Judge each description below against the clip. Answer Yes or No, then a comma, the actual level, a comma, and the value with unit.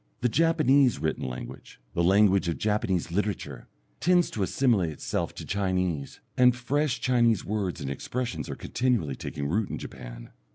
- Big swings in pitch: Yes, wide, 6.9 semitones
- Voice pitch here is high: No, low, 105 Hz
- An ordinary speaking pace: Yes, average, 155 wpm